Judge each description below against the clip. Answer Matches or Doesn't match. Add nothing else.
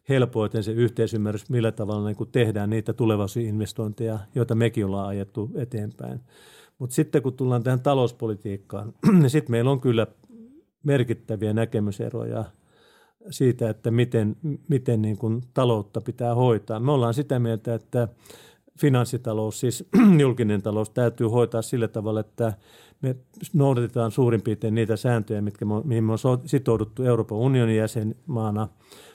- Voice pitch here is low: Matches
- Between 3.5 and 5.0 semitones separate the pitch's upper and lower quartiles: Doesn't match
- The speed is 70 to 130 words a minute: Doesn't match